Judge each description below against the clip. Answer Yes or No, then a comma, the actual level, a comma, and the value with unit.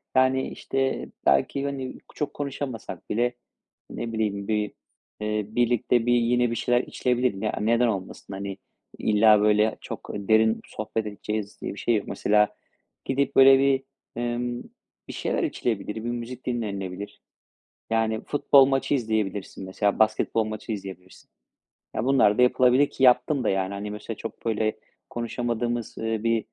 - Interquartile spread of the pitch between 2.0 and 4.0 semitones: Yes, average, 2.8 semitones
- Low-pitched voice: Yes, low, 115 Hz